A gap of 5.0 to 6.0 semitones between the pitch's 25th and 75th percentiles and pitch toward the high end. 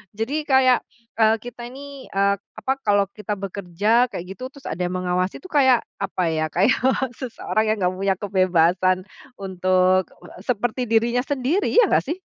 Yes: wide, 5.4 semitones; high, 215 Hz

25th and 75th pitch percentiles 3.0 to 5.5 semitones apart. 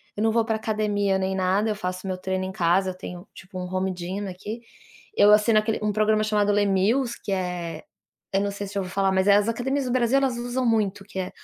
No: narrow, 2.5 semitones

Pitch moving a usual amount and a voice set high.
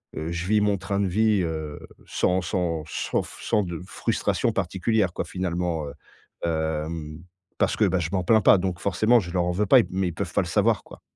No: average, 3.0 semitones; very low, 90 Hz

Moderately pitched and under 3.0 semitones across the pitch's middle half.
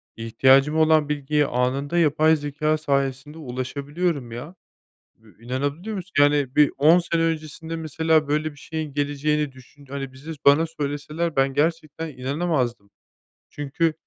Yes: medium, 145 Hz; narrow, 2.5 semitones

